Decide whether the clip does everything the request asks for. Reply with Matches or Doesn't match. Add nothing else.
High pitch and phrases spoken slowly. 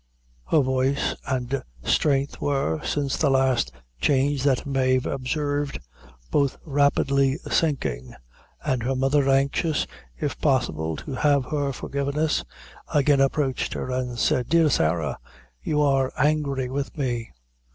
Doesn't match